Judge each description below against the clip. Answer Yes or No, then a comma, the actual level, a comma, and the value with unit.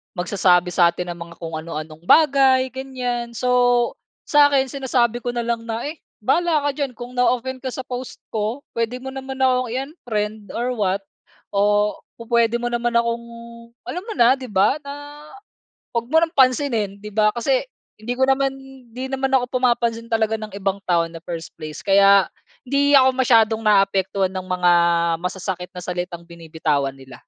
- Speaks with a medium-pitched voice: No, high, 235 Hz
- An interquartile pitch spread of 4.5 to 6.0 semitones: Yes, average, 5.1 semitones